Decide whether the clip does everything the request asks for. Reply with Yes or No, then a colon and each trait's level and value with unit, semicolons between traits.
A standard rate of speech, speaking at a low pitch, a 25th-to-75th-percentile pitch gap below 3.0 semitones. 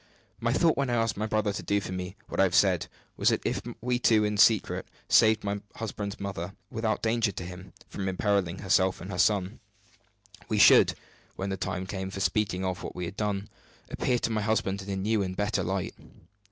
No: fast, 215 wpm; low, 100 Hz; narrow, 2.6 semitones